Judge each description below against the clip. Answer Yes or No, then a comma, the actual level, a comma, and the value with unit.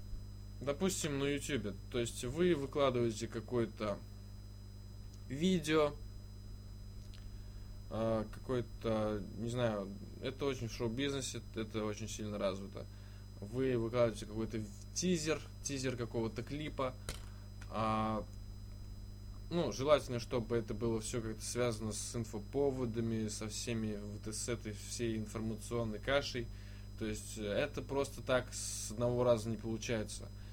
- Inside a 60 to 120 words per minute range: Yes, slow, 110 wpm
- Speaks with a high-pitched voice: No, low, 110 Hz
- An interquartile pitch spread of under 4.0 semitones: Yes, average, 3.1 semitones